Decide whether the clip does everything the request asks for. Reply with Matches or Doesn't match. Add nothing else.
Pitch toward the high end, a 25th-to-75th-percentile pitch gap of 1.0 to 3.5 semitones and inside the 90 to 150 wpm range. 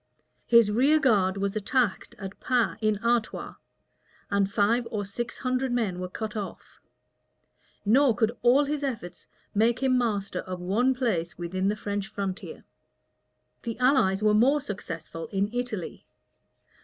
Doesn't match